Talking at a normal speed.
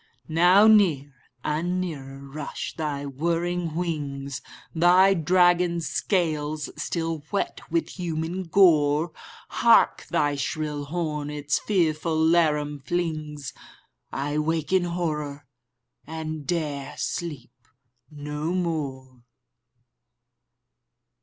No: slow, 95 wpm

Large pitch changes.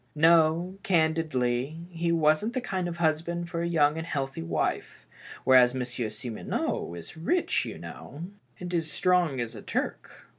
No: average, 4.7 semitones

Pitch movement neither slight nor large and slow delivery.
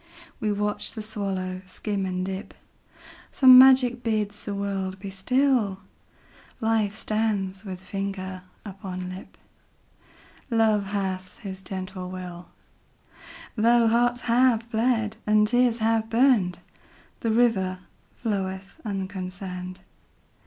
Yes: average, 3.2 semitones; slow, 95 wpm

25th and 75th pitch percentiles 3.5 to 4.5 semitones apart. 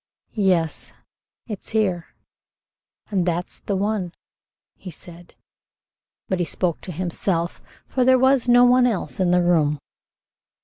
Yes: average, 4.0 semitones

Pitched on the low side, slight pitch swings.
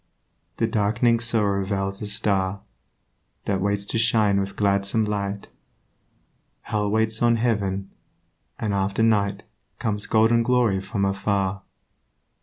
Yes: low, 100 Hz; narrow, 2.1 semitones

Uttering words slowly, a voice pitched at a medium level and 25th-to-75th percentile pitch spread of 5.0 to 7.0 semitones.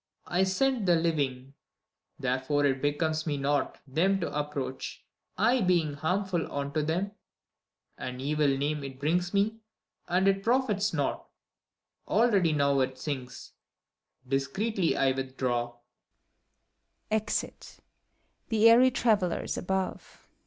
Yes: slow, 100 wpm; medium, 150 Hz; wide, 5.6 semitones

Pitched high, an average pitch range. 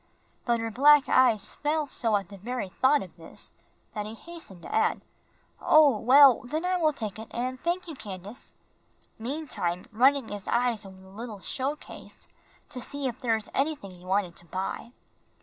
No: high, 240 Hz; wide, 5.9 semitones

